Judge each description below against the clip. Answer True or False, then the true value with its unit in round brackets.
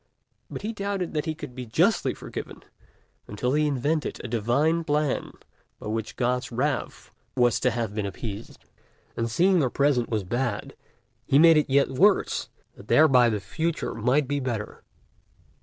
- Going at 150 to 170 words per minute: True (160 wpm)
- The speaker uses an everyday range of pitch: True (4.7 semitones)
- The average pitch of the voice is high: False (130 Hz)